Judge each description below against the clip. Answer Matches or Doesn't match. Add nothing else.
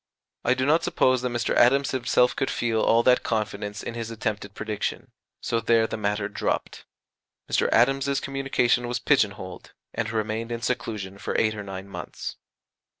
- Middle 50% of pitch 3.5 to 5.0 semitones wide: Doesn't match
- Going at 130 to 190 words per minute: Matches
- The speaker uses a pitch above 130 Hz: Doesn't match